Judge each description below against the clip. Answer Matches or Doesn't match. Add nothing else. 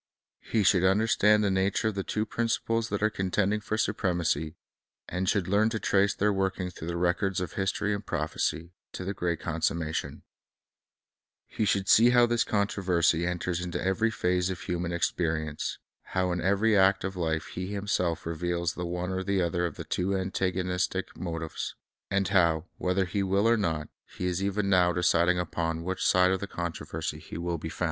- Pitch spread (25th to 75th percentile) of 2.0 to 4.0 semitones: Matches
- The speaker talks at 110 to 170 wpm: Doesn't match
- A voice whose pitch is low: Matches